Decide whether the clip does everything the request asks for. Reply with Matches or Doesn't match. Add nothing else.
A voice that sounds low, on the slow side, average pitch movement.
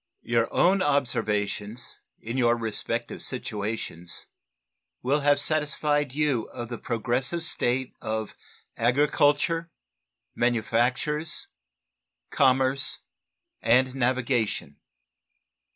Matches